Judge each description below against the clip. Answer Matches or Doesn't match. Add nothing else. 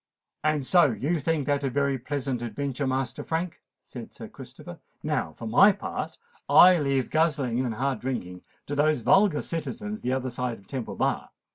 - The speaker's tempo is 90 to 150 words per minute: Doesn't match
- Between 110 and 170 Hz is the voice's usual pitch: Matches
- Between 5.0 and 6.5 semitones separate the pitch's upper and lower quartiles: Doesn't match